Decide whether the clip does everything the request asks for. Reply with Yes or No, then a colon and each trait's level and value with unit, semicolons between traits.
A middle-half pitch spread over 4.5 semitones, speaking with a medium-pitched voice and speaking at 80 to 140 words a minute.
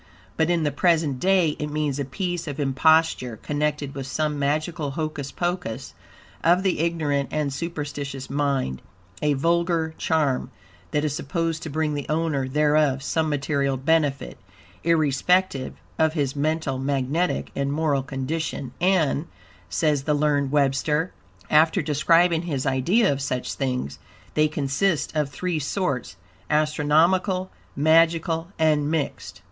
No: average, 2.8 semitones; medium, 150 Hz; slow, 135 wpm